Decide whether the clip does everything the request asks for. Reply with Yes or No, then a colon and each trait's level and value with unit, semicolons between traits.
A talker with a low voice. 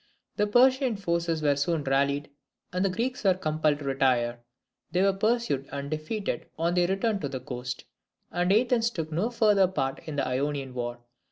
No: medium, 165 Hz